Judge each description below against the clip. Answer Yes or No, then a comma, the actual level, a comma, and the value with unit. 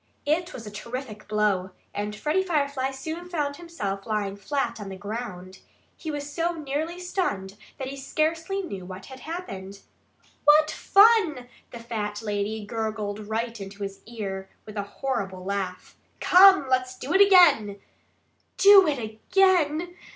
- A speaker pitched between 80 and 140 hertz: No, high, 245 Hz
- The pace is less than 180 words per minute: Yes, average, 150 wpm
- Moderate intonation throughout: No, wide, 7.7 semitones